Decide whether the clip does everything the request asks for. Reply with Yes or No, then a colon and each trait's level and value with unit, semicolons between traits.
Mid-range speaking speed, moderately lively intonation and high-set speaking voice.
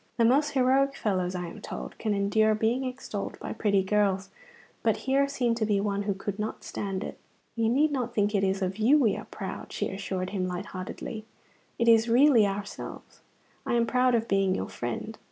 No: fast, 210 wpm; average, 3.6 semitones; high, 215 Hz